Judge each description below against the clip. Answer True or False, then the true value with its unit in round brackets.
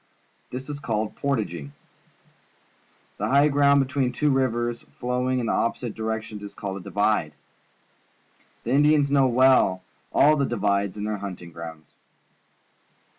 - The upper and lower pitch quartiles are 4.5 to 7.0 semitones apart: True (5.1 semitones)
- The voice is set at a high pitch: False (120 Hz)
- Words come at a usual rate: False (130 wpm)